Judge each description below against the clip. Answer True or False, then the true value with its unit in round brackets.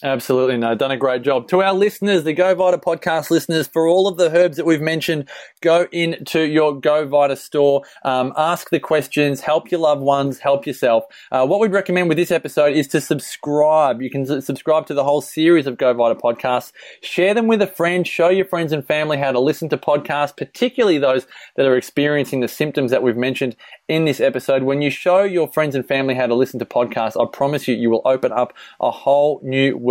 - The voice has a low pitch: False (150 Hz)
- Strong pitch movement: False (3.7 semitones)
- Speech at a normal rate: False (220 wpm)